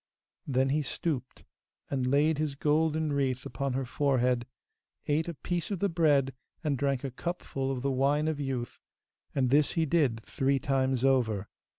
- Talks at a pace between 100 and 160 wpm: No, average, 170 wpm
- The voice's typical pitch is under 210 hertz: Yes, medium, 140 Hz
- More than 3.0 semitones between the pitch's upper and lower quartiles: No, average, 2.7 semitones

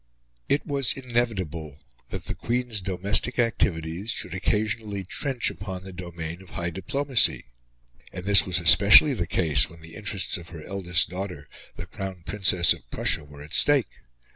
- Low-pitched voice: Yes, very low, 95 Hz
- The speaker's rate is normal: Yes, average, 160 wpm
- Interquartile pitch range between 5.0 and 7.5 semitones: No, average, 4.3 semitones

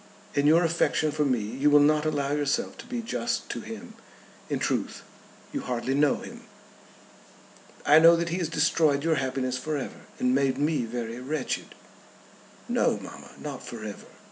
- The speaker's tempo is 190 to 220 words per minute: No, average, 170 wpm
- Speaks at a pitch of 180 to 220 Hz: No, medium, 145 Hz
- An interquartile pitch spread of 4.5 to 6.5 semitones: No, average, 3.7 semitones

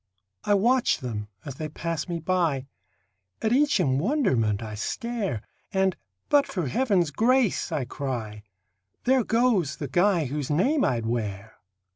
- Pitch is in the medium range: Yes, medium, 165 Hz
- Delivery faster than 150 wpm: No, average, 145 wpm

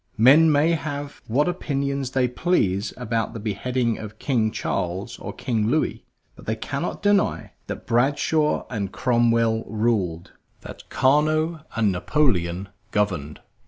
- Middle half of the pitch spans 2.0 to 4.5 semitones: No, wide, 5.5 semitones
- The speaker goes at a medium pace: No, slow, 130 wpm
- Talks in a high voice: No, low, 120 Hz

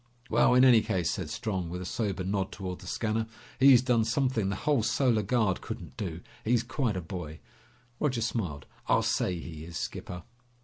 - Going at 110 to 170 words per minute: No, average, 185 wpm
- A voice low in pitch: Yes, low, 105 Hz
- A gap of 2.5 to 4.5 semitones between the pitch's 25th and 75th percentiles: No, average, 5.0 semitones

